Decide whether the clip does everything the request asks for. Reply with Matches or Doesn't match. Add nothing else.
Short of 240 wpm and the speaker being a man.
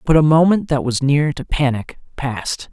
Matches